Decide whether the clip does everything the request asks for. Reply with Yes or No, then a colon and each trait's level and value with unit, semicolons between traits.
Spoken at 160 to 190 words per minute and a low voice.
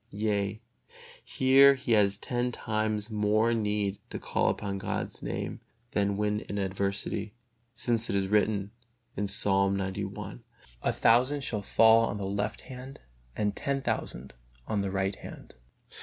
No: average, 140 wpm; low, 105 Hz